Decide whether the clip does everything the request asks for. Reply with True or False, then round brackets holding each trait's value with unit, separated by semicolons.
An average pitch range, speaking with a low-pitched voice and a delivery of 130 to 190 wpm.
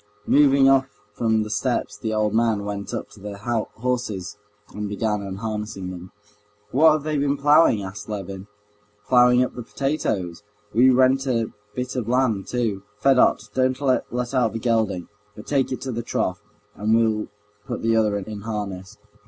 True (3.8 semitones; 115 Hz; 170 wpm)